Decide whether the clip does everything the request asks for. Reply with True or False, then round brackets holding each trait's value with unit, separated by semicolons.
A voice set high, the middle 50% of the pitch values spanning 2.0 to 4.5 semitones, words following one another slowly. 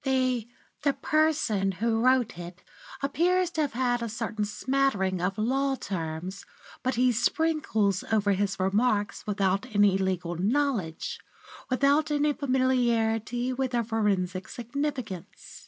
False (230 Hz; 5.2 semitones; 125 wpm)